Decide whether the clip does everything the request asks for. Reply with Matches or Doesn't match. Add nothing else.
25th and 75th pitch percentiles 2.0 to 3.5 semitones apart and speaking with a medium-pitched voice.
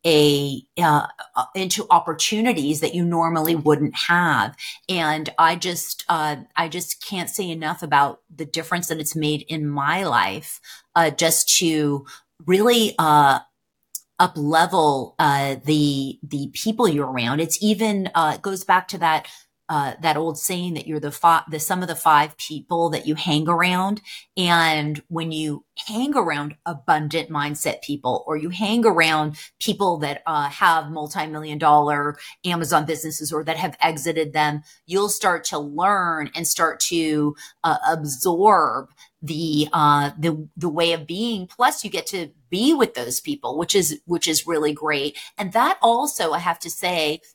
Matches